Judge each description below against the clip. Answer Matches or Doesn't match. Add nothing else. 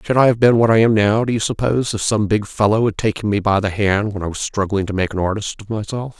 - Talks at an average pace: Doesn't match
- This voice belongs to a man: Matches